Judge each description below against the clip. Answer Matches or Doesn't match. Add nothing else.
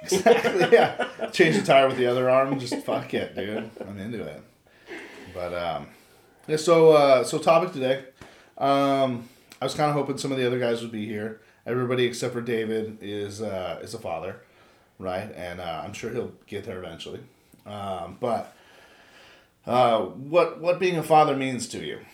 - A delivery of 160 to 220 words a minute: Matches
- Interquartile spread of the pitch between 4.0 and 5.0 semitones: Matches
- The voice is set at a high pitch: Doesn't match